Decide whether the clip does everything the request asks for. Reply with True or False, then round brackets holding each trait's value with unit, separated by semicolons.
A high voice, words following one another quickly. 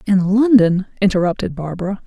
False (195 Hz; 115 wpm)